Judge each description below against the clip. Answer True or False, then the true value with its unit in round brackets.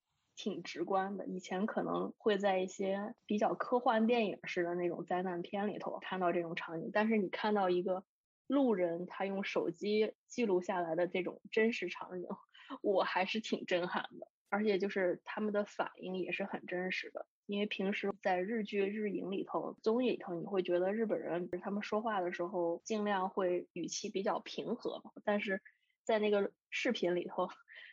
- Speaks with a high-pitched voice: True (200 Hz)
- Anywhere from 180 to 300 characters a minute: True (270 characters per minute)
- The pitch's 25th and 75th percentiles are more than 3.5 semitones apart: False (3.1 semitones)